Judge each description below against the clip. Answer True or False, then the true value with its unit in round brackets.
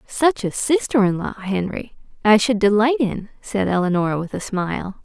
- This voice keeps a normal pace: True (180 wpm)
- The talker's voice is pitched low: False (210 Hz)